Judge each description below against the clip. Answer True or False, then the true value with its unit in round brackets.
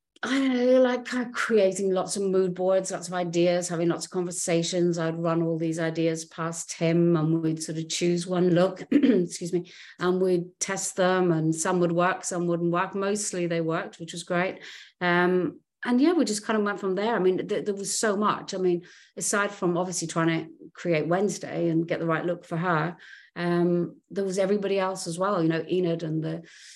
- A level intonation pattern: True (2.3 semitones)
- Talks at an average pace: False (215 wpm)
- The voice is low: False (180 Hz)